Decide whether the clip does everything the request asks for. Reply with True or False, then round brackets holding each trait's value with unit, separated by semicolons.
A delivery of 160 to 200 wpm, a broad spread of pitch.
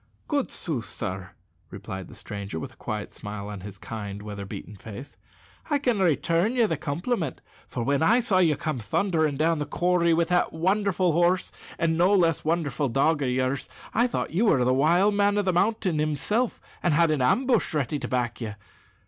True (195 wpm; 6.8 semitones)